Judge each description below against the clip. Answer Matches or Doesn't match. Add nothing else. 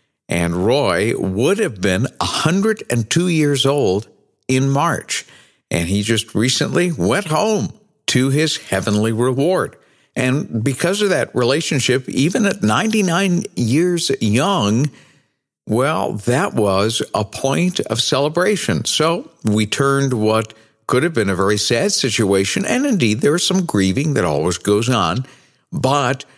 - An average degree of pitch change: Doesn't match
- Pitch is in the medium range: Doesn't match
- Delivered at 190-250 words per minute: Doesn't match